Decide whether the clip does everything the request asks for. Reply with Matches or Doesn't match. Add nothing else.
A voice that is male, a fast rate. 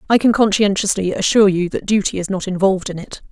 Doesn't match